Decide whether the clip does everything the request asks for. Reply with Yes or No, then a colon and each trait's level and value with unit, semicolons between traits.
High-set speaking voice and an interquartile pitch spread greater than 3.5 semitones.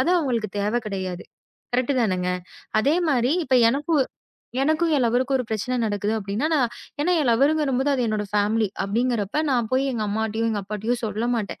Yes: high, 235 Hz; average, 3.9 semitones